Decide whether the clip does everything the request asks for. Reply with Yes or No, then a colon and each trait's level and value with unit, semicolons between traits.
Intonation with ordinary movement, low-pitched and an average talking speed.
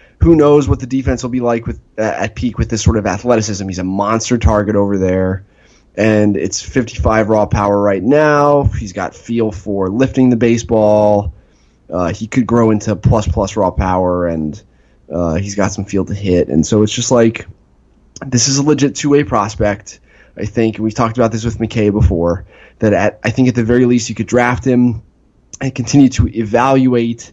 Yes: average, 3.4 semitones; low, 110 Hz; average, 195 wpm